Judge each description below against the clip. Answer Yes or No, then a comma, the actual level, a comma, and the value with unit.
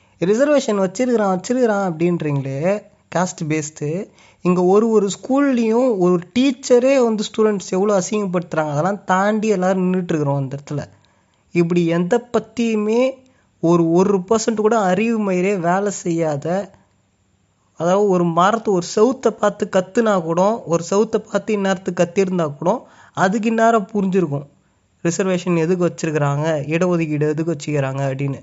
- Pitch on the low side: No, medium, 185 Hz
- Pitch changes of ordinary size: Yes, average, 4.3 semitones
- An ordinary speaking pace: Yes, average, 120 wpm